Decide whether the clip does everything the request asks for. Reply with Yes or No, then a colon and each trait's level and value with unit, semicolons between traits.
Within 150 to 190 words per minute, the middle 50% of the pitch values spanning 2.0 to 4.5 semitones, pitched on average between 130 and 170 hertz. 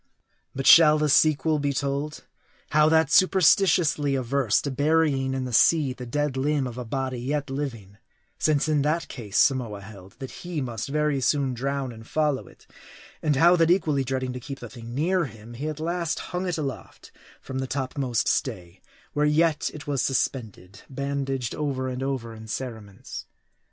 Yes: average, 175 wpm; average, 3.2 semitones; medium, 140 Hz